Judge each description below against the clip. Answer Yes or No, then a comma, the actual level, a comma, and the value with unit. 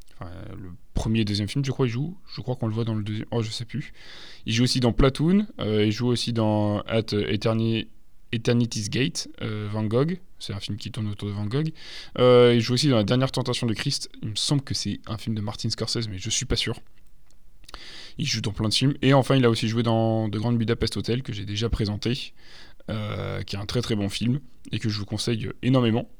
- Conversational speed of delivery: No, fast, 245 wpm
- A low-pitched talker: Yes, low, 115 Hz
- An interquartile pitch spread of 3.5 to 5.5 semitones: No, average, 2.7 semitones